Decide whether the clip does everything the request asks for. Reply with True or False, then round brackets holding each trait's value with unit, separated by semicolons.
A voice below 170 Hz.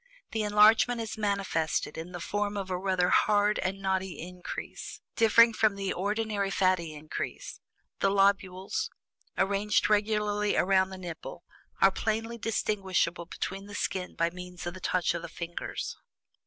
False (195 Hz)